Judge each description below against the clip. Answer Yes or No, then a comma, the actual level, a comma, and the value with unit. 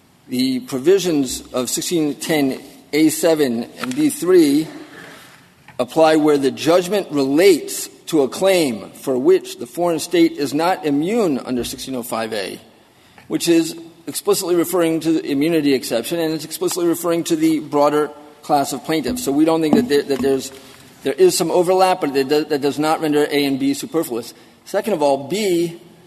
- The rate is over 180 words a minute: No, average, 150 wpm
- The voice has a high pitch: No, medium, 160 Hz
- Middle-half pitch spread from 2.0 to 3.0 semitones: No, average, 4.0 semitones